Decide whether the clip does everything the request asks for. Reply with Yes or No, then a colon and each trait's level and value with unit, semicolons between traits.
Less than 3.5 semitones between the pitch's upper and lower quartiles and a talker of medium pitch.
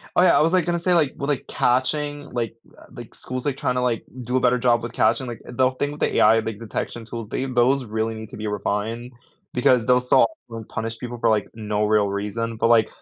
No: narrow, 2.6 semitones; low, 120 Hz